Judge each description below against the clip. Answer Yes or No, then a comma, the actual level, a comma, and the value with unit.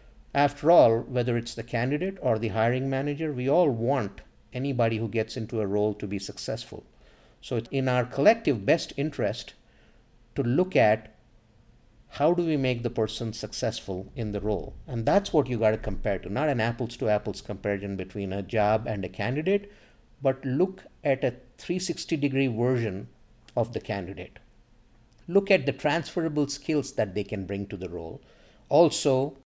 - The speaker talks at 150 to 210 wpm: Yes, average, 175 wpm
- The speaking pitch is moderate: No, low, 115 Hz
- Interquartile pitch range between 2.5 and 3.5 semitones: No, average, 4.6 semitones